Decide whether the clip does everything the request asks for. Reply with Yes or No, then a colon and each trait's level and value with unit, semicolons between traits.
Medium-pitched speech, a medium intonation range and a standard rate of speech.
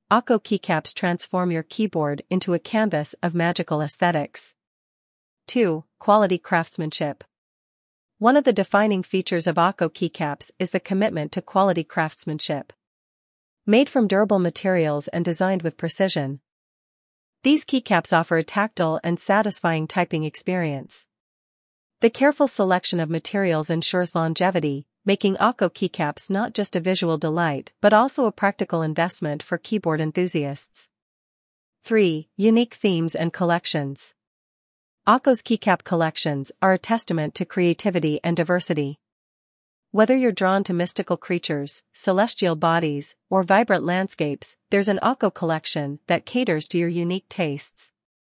No: medium, 175 Hz; average, 4.0 semitones; slow, 130 wpm